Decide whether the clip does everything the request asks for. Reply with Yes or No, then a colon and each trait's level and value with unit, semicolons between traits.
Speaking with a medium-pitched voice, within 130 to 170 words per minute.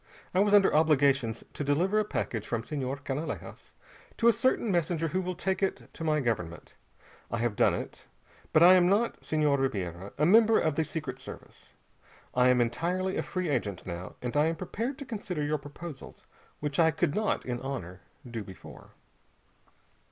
No: medium, 150 Hz; average, 180 wpm